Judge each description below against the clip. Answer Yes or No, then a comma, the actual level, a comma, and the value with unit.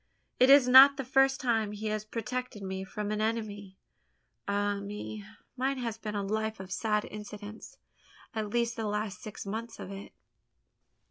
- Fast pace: No, average, 170 wpm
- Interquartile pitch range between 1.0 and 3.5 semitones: Yes, narrow, 2.4 semitones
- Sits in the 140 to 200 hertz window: No, high, 215 Hz